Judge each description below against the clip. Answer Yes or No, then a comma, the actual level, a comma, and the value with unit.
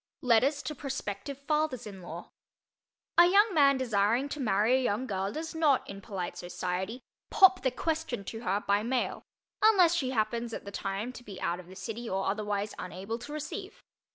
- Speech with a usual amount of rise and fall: No, wide, 6.4 semitones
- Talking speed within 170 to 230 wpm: Yes, average, 185 wpm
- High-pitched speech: Yes, high, 235 Hz